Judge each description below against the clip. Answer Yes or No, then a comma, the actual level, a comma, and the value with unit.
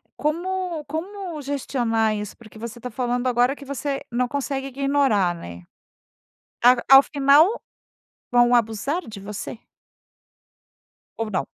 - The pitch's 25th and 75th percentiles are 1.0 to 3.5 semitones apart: No, average, 4.1 semitones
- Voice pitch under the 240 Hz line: No, very high, 255 Hz